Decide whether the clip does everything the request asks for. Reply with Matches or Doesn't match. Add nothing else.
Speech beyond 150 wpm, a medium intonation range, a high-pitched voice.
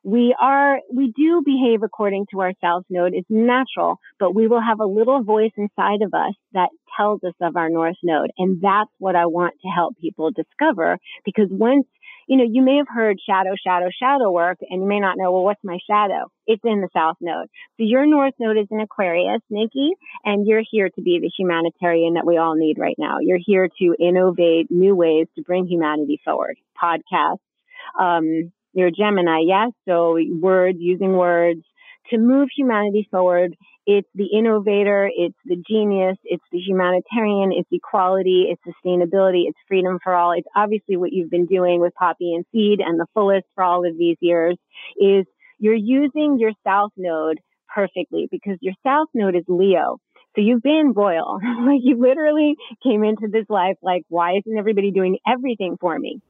Matches